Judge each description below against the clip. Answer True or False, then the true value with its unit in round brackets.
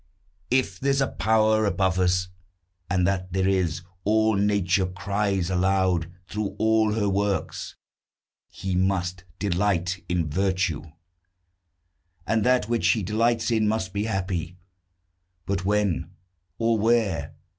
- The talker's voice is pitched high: False (100 Hz)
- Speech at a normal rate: False (125 wpm)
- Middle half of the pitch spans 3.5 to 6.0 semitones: False (3.0 semitones)